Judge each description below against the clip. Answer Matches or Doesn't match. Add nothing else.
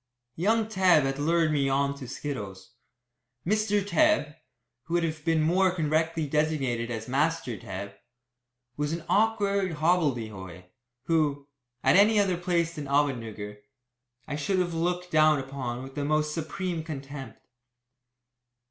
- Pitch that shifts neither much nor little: Matches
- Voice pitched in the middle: Matches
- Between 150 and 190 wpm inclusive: Doesn't match